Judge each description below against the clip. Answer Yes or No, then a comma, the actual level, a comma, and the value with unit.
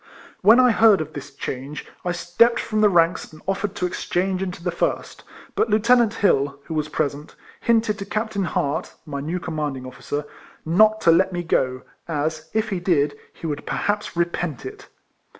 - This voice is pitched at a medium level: Yes, medium, 175 Hz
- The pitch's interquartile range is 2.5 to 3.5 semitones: No, wide, 5.5 semitones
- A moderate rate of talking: Yes, average, 185 wpm